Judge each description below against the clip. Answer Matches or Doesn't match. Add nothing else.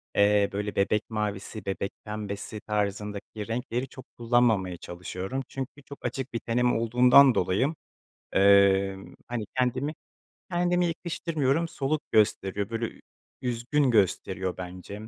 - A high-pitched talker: Doesn't match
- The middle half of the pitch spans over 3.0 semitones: Matches